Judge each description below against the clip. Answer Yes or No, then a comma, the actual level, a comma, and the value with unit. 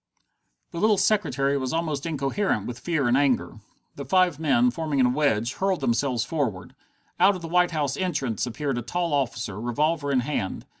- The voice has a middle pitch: Yes, medium, 145 Hz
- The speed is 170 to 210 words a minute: Yes, average, 180 wpm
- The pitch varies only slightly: No, average, 5.2 semitones